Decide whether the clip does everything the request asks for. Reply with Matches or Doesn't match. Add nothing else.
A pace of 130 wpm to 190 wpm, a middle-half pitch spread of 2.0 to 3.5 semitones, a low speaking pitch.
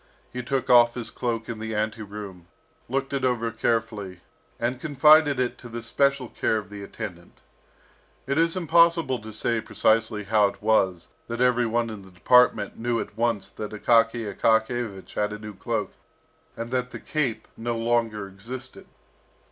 Matches